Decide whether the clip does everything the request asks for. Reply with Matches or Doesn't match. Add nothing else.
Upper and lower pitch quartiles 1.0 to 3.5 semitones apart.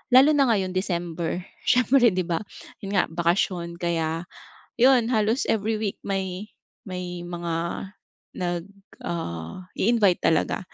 Doesn't match